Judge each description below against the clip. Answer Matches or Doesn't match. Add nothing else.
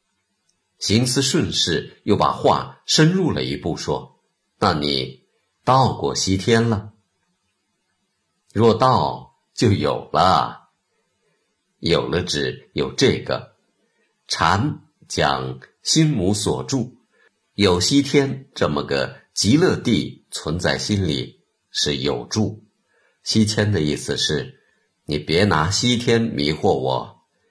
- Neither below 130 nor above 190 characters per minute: Matches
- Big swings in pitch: Matches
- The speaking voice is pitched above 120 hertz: Doesn't match